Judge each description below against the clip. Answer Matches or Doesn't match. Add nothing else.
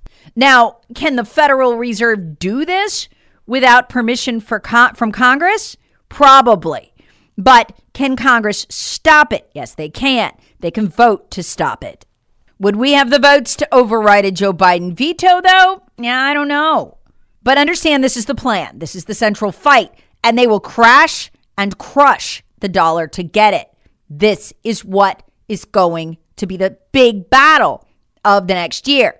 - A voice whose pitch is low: Doesn't match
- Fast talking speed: Doesn't match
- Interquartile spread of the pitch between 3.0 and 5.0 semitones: Doesn't match